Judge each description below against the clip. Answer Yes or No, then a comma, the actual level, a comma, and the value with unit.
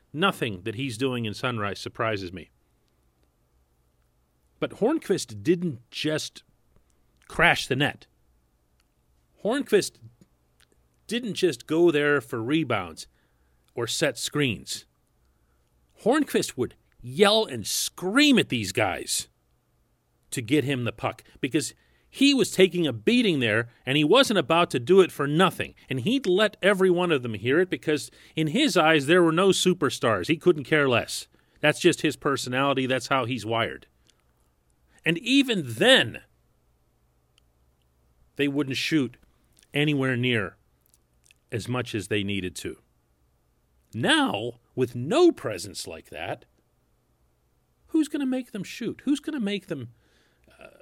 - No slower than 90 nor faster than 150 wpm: Yes, slow, 135 wpm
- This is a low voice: Yes, low, 125 Hz